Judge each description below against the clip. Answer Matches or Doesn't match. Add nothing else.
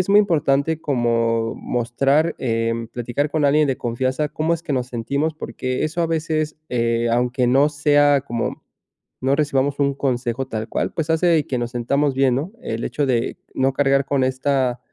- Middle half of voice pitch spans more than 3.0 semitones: Matches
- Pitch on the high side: Doesn't match